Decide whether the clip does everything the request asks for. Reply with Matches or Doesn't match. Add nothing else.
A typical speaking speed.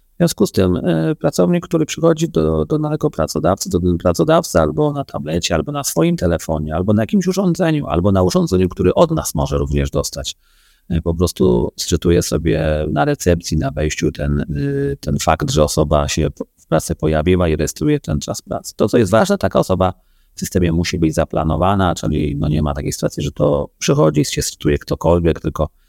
Doesn't match